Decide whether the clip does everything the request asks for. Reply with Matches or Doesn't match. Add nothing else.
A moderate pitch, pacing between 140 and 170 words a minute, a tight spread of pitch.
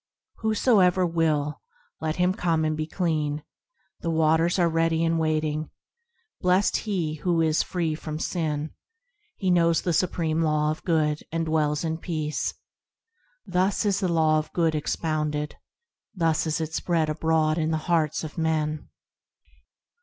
Matches